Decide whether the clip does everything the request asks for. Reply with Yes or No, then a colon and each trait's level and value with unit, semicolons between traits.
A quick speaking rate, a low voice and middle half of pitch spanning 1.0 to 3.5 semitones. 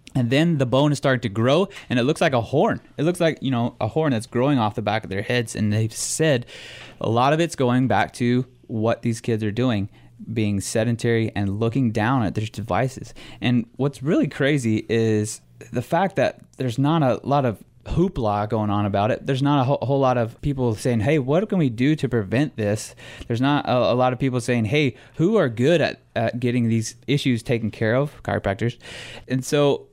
No: fast, 215 wpm; low, 125 Hz; average, 3.9 semitones